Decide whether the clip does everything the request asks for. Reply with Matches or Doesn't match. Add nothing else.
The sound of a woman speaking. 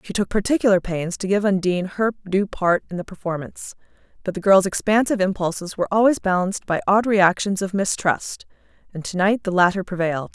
Matches